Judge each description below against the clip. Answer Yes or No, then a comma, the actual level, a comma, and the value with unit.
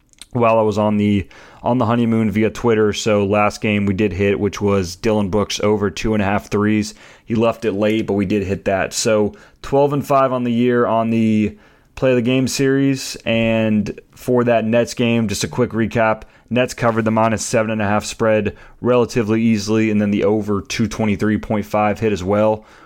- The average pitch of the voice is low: Yes, low, 110 Hz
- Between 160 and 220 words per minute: Yes, average, 200 wpm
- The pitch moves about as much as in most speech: No, narrow, 2.1 semitones